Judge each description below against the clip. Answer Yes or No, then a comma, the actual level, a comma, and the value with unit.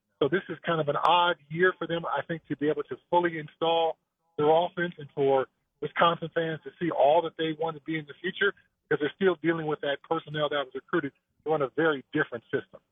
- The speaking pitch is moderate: Yes, medium, 160 Hz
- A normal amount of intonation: No, narrow, 2.1 semitones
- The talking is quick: Yes, fast, 230 wpm